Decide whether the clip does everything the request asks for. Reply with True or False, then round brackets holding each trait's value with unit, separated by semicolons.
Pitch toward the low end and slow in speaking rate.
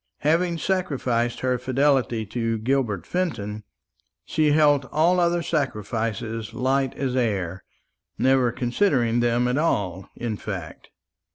True (125 Hz; 115 wpm)